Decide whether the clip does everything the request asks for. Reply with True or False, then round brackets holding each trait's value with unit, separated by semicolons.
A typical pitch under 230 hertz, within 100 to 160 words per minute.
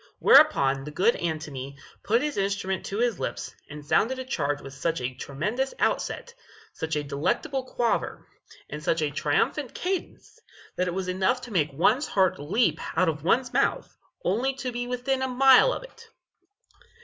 False (190 Hz; 175 wpm)